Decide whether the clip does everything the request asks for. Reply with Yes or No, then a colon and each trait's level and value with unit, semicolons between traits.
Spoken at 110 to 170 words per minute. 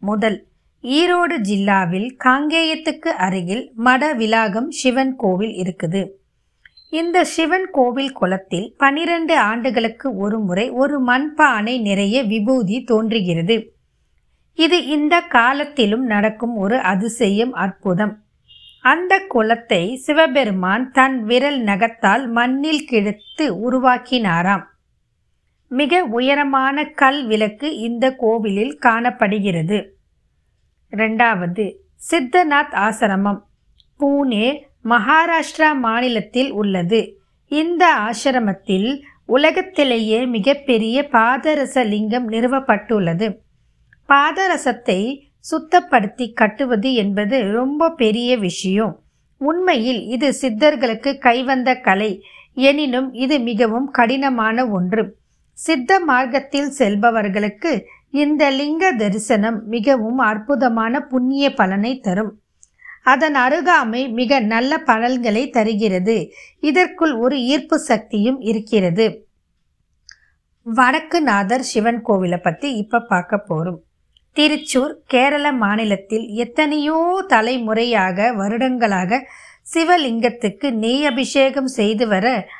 No: average, 85 wpm